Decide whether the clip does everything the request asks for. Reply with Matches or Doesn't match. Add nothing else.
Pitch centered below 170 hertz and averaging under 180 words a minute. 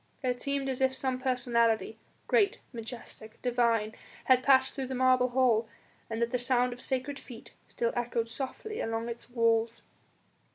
Doesn't match